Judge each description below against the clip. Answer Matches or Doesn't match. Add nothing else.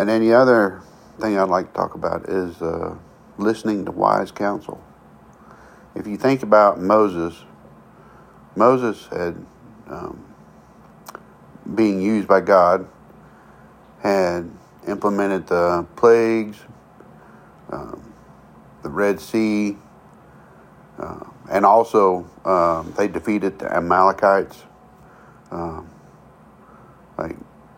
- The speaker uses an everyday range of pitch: Matches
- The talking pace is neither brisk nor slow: Doesn't match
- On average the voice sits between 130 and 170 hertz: Doesn't match